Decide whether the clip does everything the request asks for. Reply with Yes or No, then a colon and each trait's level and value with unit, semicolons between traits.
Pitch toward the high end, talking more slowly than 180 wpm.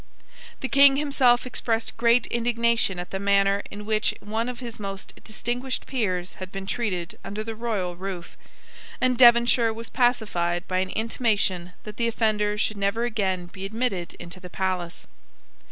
Yes: high, 215 Hz; average, 160 wpm